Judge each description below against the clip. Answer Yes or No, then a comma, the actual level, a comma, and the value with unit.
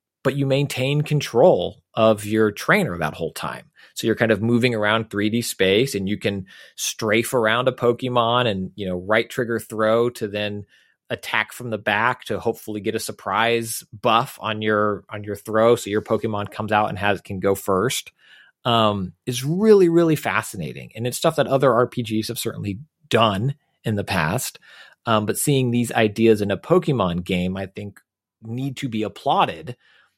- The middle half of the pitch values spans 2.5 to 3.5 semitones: Yes, average, 3.1 semitones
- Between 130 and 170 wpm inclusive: No, average, 180 wpm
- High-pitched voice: No, low, 110 Hz